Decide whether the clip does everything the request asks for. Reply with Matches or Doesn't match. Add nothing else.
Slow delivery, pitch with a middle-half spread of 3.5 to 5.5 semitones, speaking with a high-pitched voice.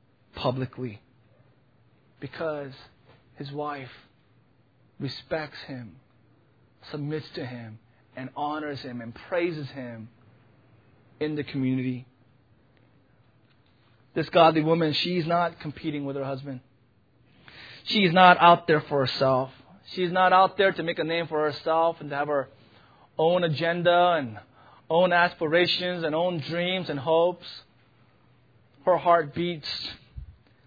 Doesn't match